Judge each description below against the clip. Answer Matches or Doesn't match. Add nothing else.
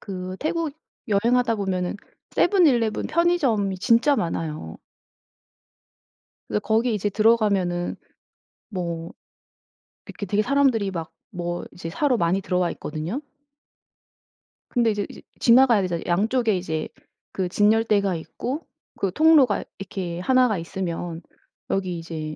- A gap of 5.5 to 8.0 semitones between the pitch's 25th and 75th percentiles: Doesn't match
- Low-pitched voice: Doesn't match